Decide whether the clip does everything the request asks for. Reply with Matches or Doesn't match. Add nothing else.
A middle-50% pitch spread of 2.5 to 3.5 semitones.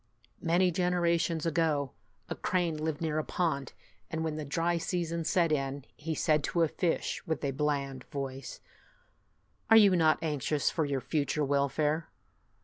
Matches